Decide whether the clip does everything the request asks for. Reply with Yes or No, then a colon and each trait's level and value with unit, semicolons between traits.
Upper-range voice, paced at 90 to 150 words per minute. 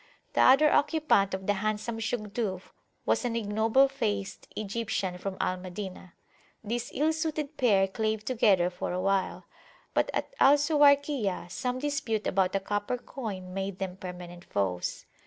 Yes: high, 210 Hz; average, 145 wpm